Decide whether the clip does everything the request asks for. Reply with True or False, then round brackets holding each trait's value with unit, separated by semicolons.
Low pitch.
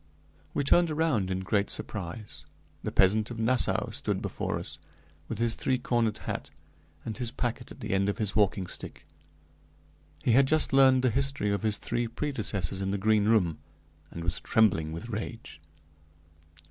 True (110 Hz)